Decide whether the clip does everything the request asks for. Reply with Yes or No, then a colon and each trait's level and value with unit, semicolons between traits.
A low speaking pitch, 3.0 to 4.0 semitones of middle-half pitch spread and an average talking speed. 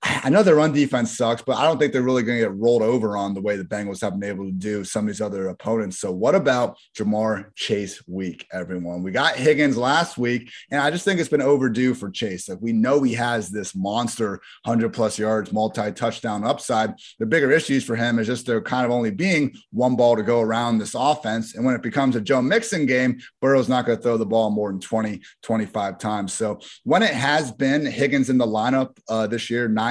No: low, 115 Hz; average, 3.3 semitones; fast, 235 wpm